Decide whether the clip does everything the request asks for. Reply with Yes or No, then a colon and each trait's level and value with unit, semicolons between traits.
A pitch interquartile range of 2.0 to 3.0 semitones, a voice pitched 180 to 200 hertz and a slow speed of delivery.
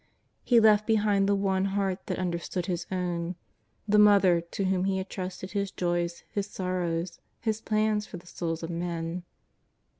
No: average, 2.7 semitones; medium, 185 Hz; average, 170 wpm